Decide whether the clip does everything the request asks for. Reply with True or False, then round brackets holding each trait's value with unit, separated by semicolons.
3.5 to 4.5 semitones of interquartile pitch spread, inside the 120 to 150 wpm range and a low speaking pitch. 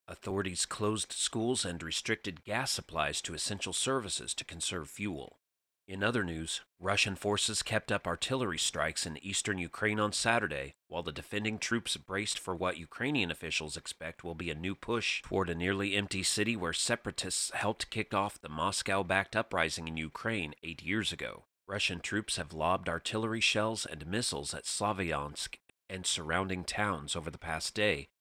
False (4.1 semitones; 165 wpm; 95 Hz)